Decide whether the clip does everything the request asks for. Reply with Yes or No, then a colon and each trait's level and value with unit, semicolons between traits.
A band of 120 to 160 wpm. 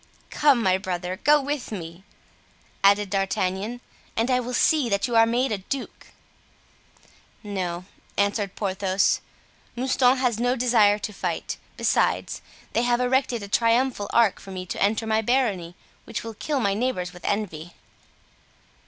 Yes: average, 150 wpm